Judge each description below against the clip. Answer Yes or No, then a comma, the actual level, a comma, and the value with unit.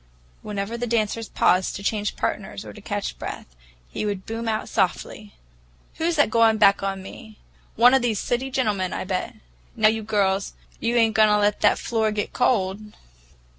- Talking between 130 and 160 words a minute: No, average, 180 wpm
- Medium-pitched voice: No, high, 215 Hz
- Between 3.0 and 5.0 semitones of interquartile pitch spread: No, narrow, 2.5 semitones